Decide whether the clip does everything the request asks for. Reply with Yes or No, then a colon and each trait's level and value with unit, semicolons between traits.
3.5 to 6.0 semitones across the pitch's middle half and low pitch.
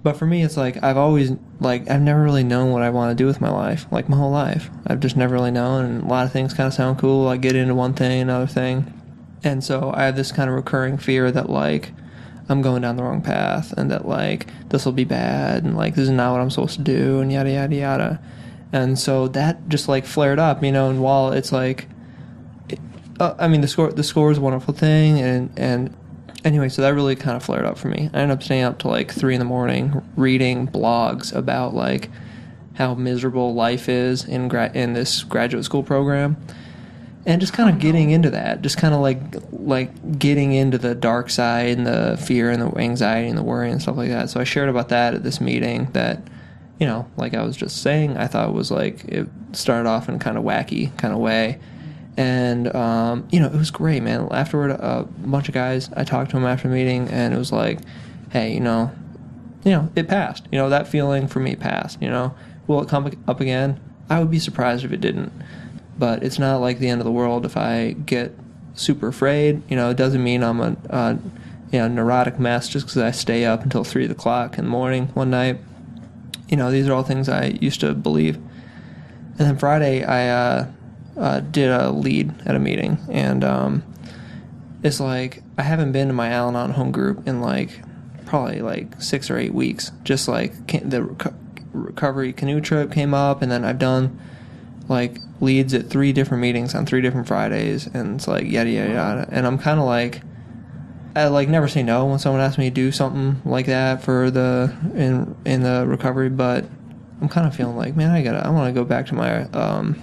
No: narrow, 2.6 semitones; low, 130 Hz